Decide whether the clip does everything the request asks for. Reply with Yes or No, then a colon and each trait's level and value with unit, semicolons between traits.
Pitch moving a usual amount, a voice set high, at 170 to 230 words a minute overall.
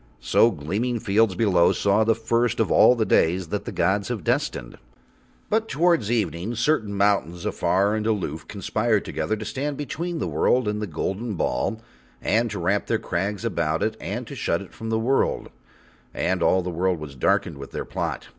No: average, 4.3 semitones; low, 105 Hz; average, 190 wpm